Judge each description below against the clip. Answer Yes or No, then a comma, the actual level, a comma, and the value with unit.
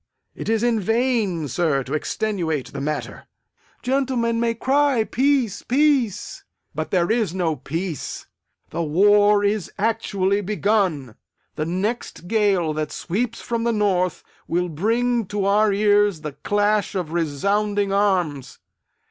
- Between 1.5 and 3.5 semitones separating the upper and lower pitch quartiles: No, average, 4.8 semitones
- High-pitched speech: Yes, high, 205 Hz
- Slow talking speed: Yes, slow, 130 wpm